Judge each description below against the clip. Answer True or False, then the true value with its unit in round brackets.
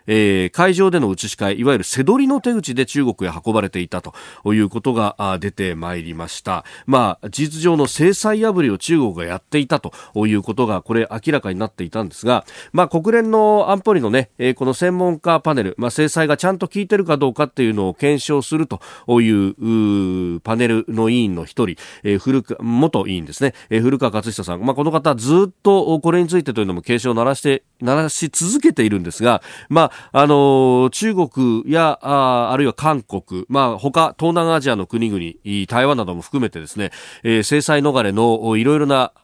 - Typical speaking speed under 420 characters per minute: True (360 characters per minute)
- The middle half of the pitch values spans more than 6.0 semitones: True (6.5 semitones)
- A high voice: False (125 Hz)